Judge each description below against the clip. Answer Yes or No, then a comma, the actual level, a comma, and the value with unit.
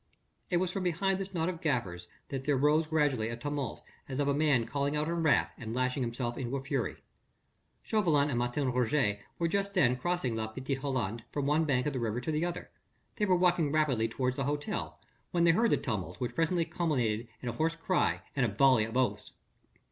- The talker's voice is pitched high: No, medium, 140 Hz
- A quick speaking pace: Yes, fast, 215 wpm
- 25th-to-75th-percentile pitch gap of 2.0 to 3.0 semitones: No, average, 4.9 semitones